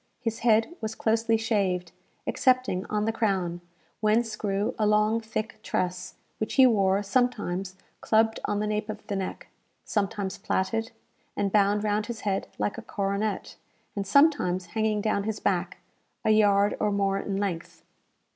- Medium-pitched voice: No, high, 210 Hz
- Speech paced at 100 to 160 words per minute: Yes, average, 155 wpm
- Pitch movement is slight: Yes, narrow, 2.0 semitones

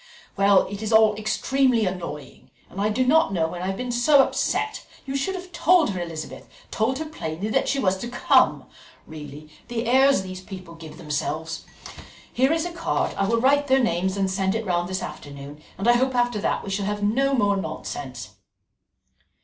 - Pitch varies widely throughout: Yes, wide, 6.6 semitones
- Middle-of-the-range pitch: No, high, 205 Hz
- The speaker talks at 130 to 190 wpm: No, average, 200 wpm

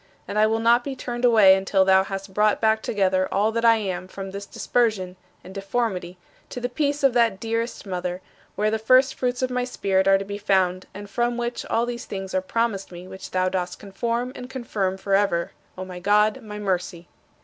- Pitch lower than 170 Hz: No, high, 205 Hz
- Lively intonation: No, average, 3.8 semitones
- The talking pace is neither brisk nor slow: No, fast, 210 wpm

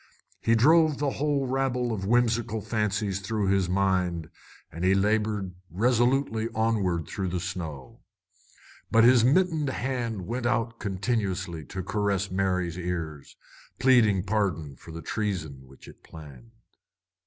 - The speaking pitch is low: Yes, low, 100 Hz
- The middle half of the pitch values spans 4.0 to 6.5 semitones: Yes, average, 4.7 semitones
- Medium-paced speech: No, slow, 130 wpm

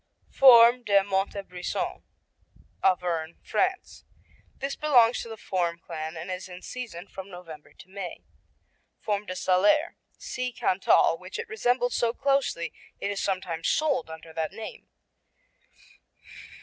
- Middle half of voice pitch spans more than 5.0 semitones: Yes, wide, 5.5 semitones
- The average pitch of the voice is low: No, high, 195 Hz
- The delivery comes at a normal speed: No, slow, 130 wpm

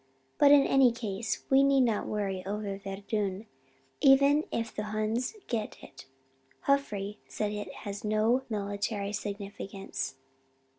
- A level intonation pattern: No, average, 3.3 semitones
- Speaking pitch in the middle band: No, high, 210 Hz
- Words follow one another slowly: Yes, slow, 130 wpm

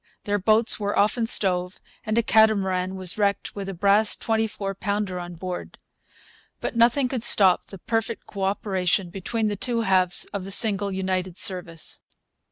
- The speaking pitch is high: Yes, high, 200 Hz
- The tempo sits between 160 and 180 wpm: Yes, average, 170 wpm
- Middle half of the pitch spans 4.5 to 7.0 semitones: No, average, 2.7 semitones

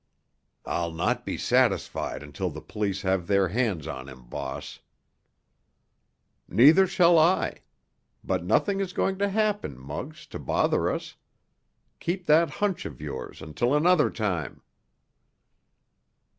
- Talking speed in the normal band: No, slow, 125 wpm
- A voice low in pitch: Yes, low, 110 Hz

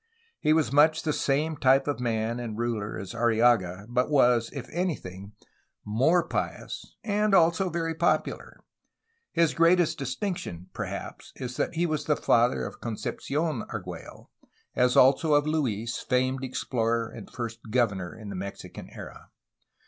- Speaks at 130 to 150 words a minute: Yes, average, 145 wpm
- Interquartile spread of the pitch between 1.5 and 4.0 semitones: No, wide, 5.6 semitones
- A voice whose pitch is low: Yes, low, 125 Hz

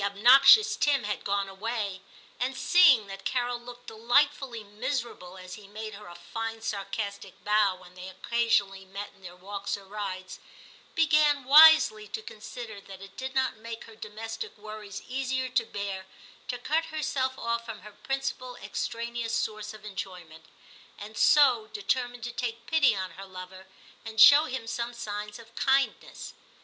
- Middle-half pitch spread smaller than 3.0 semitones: No, average, 3.8 semitones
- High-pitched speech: Yes, high, 220 Hz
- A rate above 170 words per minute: No, average, 160 wpm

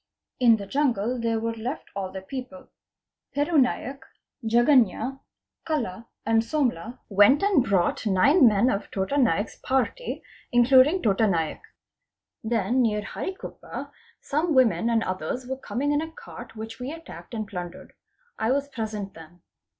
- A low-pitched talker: No, high, 235 Hz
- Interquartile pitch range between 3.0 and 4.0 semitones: No, average, 4.6 semitones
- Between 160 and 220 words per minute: No, average, 145 wpm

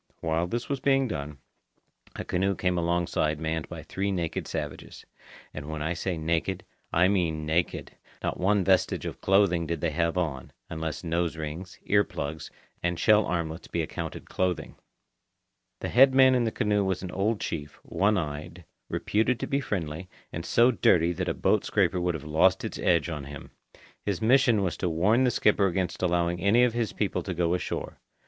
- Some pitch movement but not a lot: Yes, average, 3.8 semitones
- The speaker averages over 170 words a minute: Yes, average, 185 wpm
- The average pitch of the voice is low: Yes, very low, 90 Hz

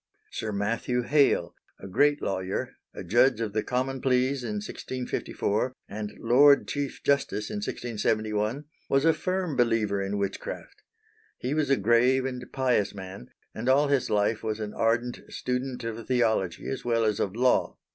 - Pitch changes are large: No, average, 3.8 semitones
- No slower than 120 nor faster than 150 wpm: No, average, 160 wpm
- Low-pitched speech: Yes, low, 120 Hz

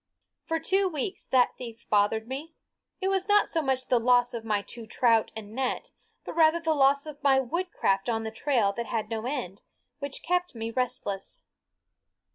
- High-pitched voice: Yes, very high, 255 Hz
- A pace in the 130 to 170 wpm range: No, average, 185 wpm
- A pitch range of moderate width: No, wide, 5.9 semitones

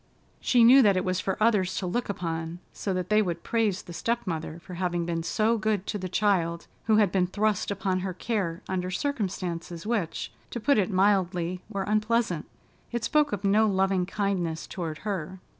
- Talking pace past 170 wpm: Yes, average, 190 wpm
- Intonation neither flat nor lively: Yes, average, 3.4 semitones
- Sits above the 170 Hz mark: Yes, high, 190 Hz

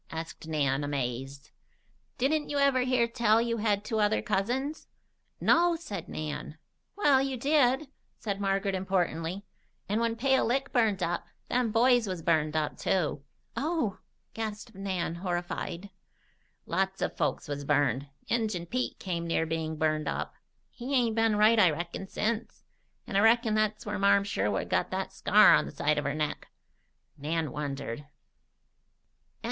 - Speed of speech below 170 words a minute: Yes, average, 155 wpm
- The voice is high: Yes, high, 200 Hz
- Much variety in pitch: Yes, wide, 6.6 semitones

